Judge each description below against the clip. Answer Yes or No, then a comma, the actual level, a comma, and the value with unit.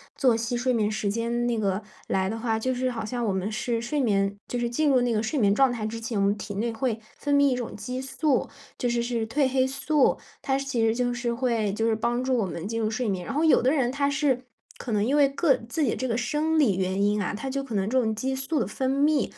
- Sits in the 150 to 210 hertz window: No, high, 240 Hz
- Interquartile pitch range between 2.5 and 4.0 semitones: Yes, average, 3.4 semitones